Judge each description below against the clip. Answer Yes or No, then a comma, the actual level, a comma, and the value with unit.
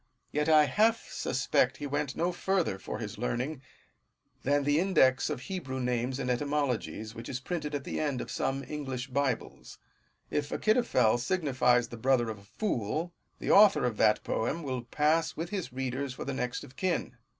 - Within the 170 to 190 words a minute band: Yes, average, 180 wpm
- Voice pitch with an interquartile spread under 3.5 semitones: No, average, 3.9 semitones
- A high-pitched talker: No, low, 135 Hz